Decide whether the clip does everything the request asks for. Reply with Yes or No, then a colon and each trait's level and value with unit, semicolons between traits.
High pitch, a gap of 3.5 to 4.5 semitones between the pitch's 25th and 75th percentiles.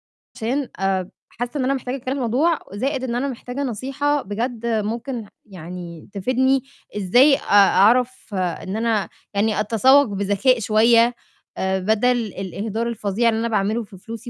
Yes: high, 230 Hz; average, 4.0 semitones